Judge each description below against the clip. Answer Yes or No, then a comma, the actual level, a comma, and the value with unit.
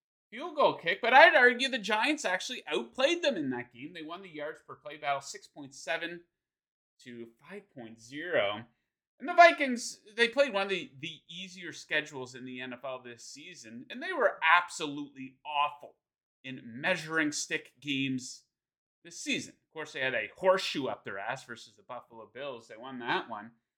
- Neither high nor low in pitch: Yes, medium, 155 Hz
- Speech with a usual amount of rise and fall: No, wide, 7.2 semitones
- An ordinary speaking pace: Yes, average, 170 wpm